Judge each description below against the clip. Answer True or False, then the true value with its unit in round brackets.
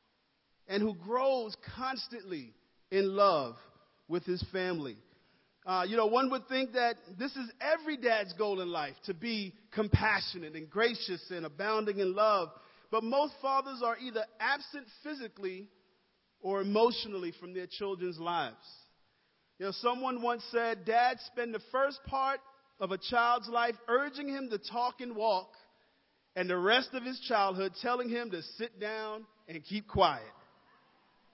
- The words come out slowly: False (150 wpm)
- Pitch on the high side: True (225 Hz)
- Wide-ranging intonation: False (4.5 semitones)